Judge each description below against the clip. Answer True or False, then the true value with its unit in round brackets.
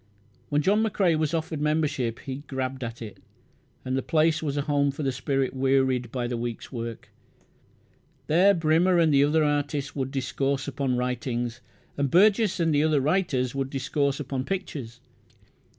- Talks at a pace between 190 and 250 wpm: False (165 wpm)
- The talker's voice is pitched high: False (140 Hz)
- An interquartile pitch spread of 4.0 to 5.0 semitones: False (3.3 semitones)